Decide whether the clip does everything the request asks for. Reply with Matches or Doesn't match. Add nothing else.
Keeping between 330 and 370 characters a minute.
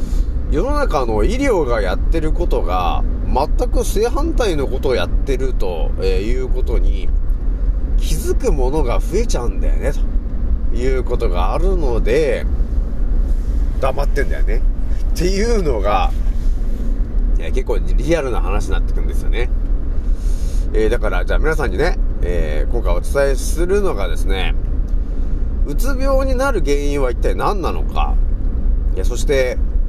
Doesn't match